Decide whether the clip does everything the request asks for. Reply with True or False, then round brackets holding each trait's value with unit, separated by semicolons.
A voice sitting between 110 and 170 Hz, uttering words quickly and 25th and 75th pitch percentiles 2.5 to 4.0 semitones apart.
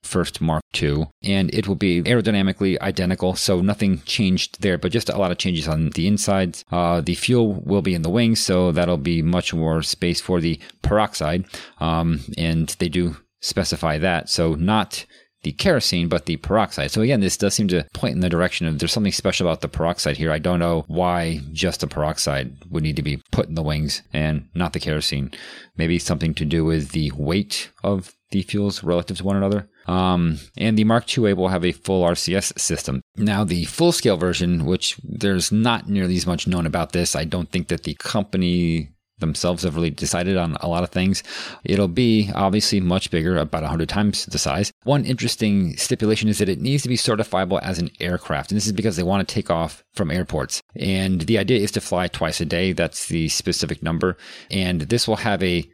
False (90 Hz; 210 wpm; 3.4 semitones)